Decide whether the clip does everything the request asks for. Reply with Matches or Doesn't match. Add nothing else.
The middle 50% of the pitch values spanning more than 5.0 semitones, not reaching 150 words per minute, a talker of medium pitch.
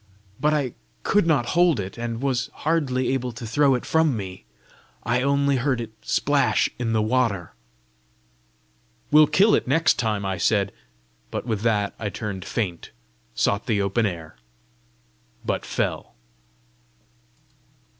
Doesn't match